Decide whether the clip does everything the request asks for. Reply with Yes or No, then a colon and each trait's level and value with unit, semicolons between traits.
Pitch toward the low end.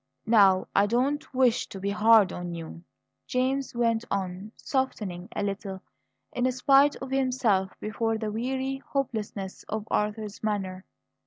No: high, 220 Hz